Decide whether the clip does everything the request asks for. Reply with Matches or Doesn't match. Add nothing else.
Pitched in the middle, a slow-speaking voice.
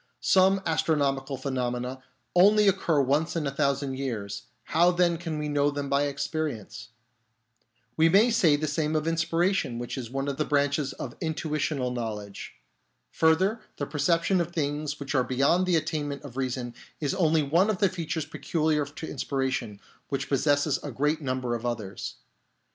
Doesn't match